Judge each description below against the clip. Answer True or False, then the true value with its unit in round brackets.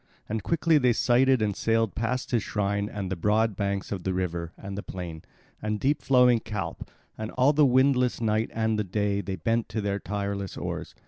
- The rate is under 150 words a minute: False (200 wpm)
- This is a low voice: True (105 Hz)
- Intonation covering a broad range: False (3.5 semitones)